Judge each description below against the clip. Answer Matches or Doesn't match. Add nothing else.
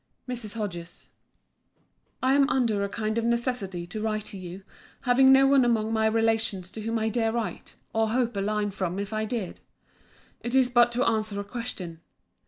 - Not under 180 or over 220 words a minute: Matches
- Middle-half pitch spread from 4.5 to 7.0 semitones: Doesn't match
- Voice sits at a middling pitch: Doesn't match